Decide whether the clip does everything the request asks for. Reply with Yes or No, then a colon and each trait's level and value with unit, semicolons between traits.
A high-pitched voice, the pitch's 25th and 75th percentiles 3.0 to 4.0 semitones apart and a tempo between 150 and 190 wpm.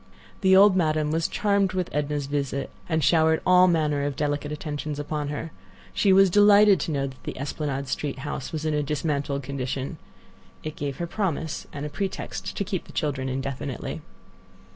No: medium, 150 Hz; average, 3.5 semitones; average, 180 wpm